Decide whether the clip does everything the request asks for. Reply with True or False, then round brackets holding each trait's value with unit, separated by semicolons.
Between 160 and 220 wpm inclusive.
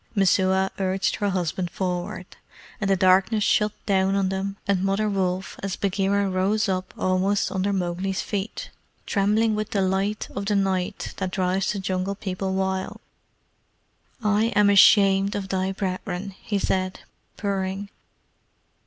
False (140 wpm)